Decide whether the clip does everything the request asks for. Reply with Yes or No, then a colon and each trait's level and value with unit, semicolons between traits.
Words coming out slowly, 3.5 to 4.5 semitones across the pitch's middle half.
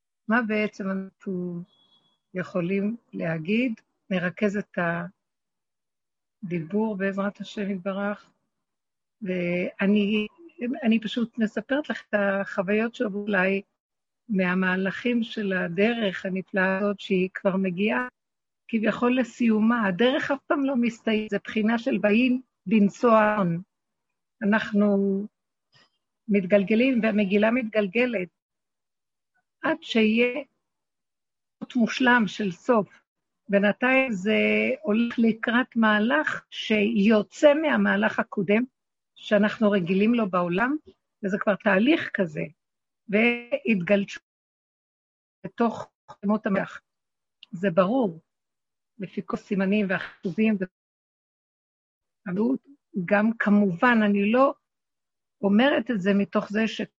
No: slow, 90 wpm; average, 3.0 semitones